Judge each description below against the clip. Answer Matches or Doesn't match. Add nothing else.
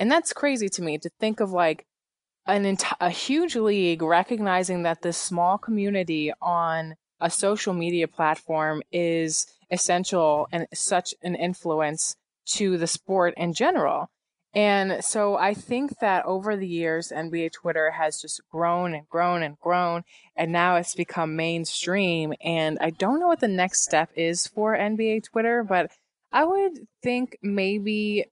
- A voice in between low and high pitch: Matches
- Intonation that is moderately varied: Matches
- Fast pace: Doesn't match